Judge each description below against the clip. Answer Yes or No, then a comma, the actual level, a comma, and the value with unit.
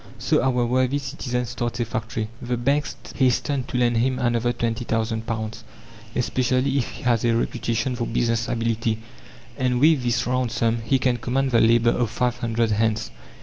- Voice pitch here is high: No, low, 120 Hz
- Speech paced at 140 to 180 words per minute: Yes, average, 170 wpm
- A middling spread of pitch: No, narrow, 1.8 semitones